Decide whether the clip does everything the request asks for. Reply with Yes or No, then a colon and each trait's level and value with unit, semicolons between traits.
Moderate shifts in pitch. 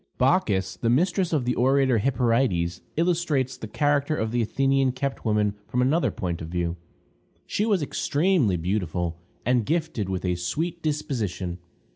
No: wide, 7.6 semitones